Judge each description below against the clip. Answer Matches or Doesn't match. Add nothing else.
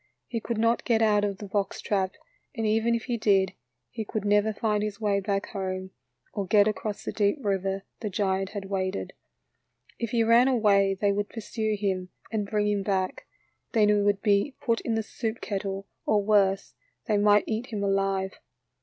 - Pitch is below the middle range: Doesn't match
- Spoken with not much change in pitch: Matches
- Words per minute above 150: Matches